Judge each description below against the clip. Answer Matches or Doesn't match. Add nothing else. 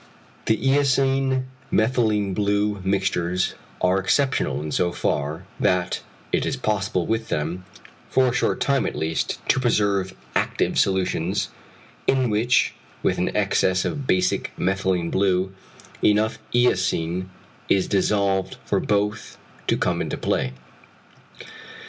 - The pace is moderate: Doesn't match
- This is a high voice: Doesn't match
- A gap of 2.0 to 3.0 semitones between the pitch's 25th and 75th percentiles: Doesn't match